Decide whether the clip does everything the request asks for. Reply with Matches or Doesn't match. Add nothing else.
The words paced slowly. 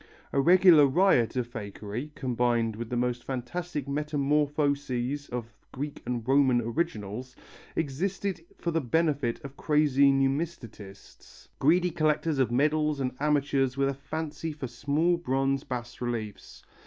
Matches